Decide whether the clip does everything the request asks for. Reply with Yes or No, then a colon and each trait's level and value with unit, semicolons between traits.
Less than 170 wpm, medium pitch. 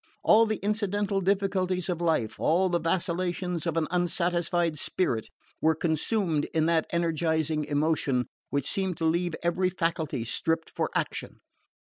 Yes: average, 140 wpm; medium, 170 Hz